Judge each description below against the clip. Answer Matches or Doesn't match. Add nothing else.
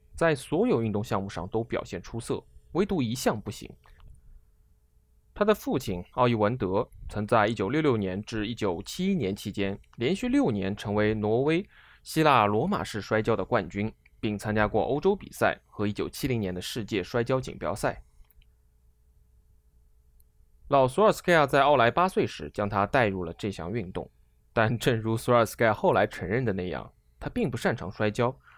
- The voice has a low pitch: Matches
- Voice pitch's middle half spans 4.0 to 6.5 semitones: Matches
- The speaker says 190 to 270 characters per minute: Matches